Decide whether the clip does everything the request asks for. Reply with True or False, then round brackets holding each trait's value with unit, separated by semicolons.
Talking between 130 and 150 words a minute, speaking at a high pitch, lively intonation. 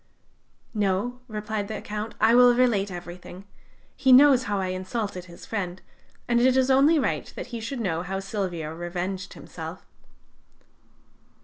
False (145 wpm; 210 Hz; 4.7 semitones)